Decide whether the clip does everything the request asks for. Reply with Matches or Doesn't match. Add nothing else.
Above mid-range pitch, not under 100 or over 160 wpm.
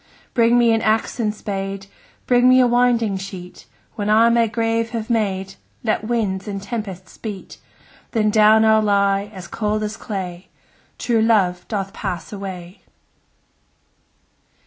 Matches